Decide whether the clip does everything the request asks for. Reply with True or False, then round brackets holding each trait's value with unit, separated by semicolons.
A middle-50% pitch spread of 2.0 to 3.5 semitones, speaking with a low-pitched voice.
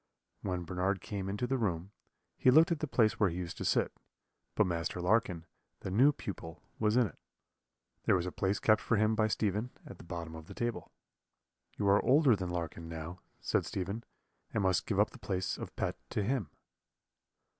False (3.9 semitones; 100 Hz)